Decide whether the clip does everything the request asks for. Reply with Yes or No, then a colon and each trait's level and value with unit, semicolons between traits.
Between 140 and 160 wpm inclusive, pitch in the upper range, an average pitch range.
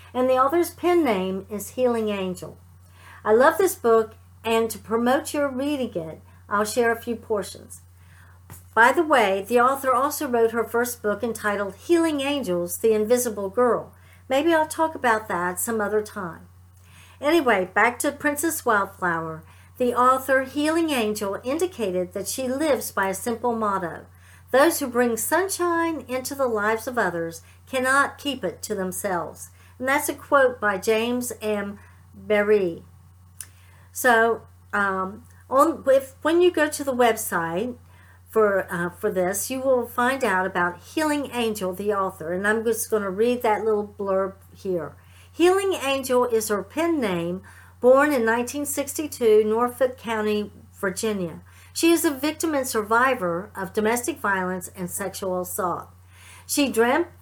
No: average, 150 wpm; high, 220 Hz; wide, 6.5 semitones